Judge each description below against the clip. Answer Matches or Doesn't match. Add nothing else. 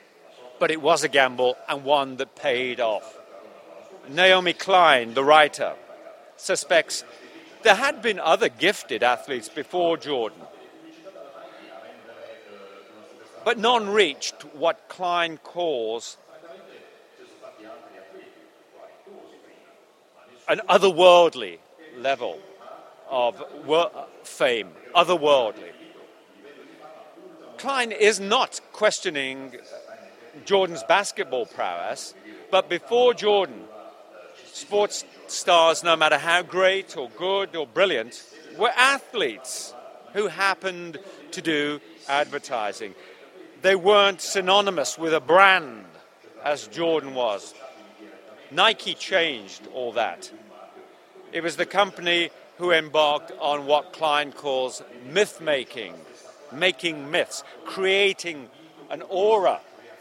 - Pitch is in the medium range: Matches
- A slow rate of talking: Matches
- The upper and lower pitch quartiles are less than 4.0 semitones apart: Doesn't match